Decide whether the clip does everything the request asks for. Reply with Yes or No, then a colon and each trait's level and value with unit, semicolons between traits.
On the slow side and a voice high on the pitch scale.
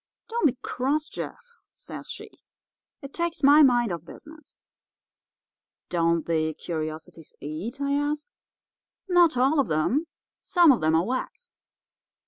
Yes: slow, 130 wpm; very high, 265 Hz